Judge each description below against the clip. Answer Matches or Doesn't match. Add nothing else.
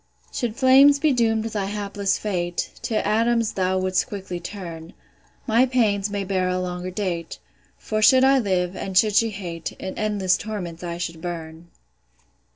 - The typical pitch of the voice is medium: Doesn't match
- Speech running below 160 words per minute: Doesn't match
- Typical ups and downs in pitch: Matches